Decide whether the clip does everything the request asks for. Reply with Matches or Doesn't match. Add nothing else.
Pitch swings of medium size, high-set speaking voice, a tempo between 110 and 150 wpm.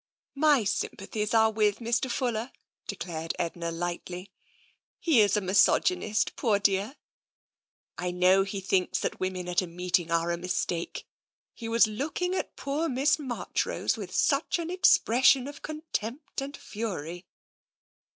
Doesn't match